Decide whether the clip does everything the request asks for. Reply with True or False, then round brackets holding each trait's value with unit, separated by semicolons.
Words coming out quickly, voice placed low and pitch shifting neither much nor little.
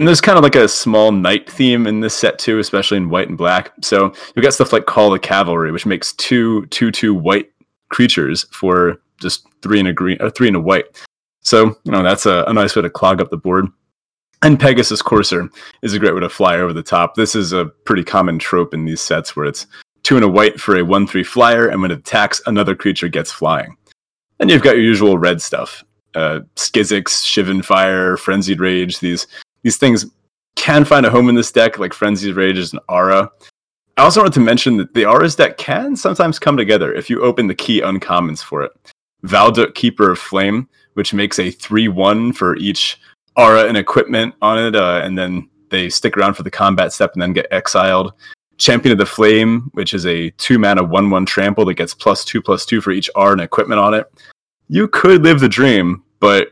True (215 wpm; 100 Hz; 4.1 semitones)